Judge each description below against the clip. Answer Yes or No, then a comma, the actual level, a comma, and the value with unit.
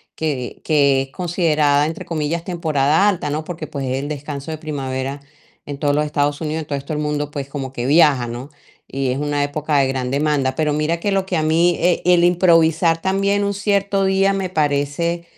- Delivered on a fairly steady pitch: No, average, 3.2 semitones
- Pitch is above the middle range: No, medium, 150 Hz